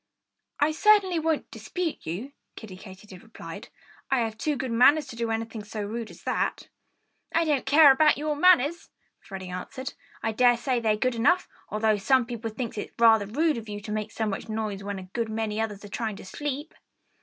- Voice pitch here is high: Yes, high, 230 Hz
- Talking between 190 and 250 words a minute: Yes, average, 200 wpm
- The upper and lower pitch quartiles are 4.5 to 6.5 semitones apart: Yes, average, 5.0 semitones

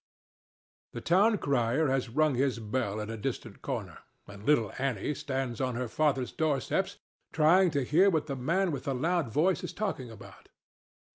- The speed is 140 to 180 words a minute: Yes, average, 170 wpm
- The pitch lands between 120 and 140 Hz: Yes, low, 135 Hz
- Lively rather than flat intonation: No, average, 4.6 semitones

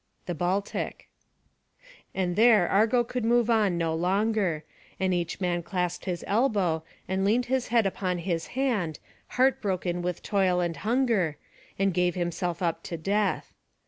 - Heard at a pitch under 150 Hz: No, high, 190 Hz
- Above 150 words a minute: No, average, 145 wpm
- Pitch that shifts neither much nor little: Yes, average, 3.9 semitones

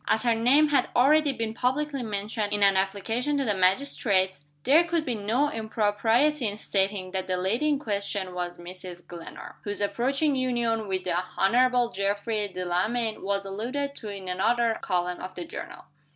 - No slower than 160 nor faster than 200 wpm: Yes, average, 170 wpm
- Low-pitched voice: No, high, 215 Hz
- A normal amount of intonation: Yes, average, 4.7 semitones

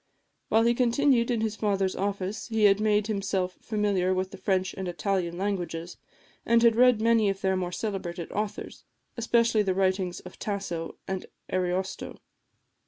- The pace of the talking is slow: No, average, 160 wpm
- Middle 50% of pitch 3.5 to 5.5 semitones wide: No, average, 2.8 semitones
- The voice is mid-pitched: No, high, 195 Hz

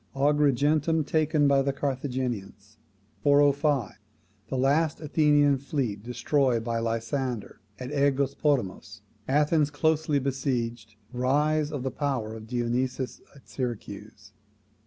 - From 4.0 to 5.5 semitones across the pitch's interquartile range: No, average, 3.2 semitones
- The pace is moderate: No, slow, 105 wpm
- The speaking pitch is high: No, low, 135 Hz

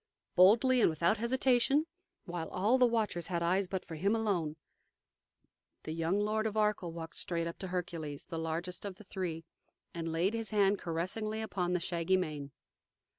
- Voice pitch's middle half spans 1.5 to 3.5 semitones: No, average, 4.3 semitones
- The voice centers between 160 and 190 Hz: Yes, medium, 185 Hz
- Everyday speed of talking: Yes, average, 175 wpm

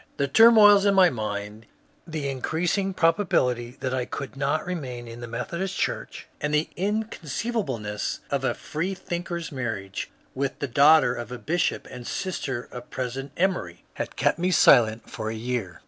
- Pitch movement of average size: No, wide, 6.7 semitones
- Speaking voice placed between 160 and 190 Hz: No, medium, 140 Hz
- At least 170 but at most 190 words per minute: No, average, 160 wpm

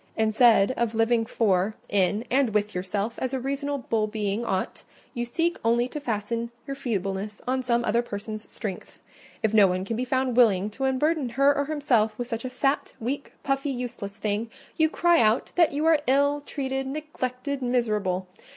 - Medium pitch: No, high, 235 Hz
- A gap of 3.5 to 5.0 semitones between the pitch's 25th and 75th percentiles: Yes, average, 4.2 semitones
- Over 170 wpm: Yes, average, 180 wpm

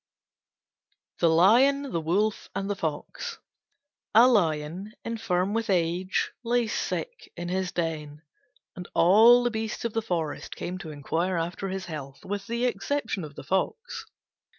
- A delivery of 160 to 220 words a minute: No, average, 150 wpm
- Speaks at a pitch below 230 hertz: Yes, high, 190 Hz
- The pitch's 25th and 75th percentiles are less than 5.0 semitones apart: No, average, 5.3 semitones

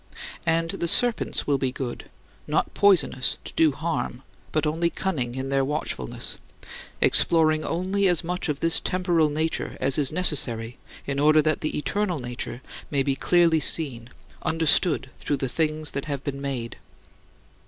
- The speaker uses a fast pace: No, average, 155 wpm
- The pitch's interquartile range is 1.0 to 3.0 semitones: No, average, 3.6 semitones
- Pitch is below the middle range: No, medium, 150 Hz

